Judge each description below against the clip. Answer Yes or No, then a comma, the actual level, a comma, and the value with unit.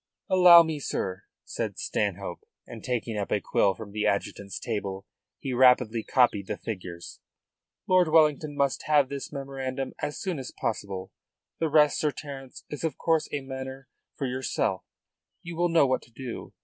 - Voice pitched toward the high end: No, low, 130 Hz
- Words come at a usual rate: Yes, average, 165 wpm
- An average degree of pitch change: No, wide, 5.8 semitones